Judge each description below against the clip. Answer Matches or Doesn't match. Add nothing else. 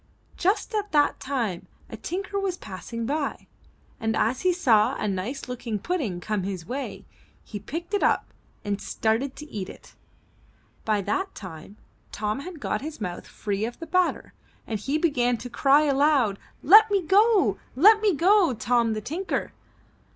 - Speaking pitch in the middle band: Doesn't match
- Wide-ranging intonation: Matches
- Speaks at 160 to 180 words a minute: Matches